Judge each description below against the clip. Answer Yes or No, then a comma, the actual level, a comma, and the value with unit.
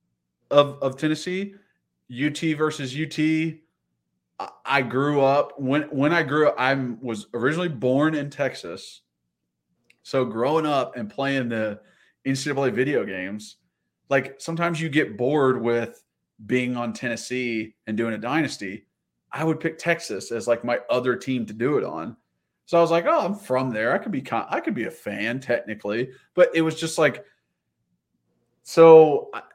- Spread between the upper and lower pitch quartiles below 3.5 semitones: No, wide, 5.6 semitones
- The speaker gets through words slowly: No, average, 165 wpm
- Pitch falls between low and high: No, low, 130 Hz